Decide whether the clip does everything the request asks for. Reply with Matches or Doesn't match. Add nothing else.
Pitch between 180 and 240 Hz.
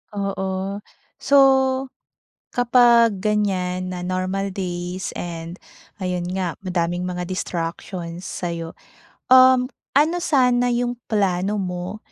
Matches